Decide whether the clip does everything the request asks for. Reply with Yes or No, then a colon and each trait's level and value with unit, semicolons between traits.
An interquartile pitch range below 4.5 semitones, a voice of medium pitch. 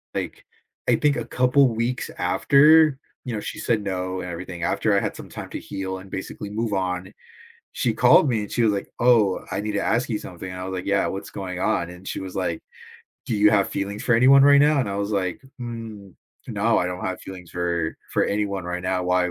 No: average, 4.0 semitones; low, 100 Hz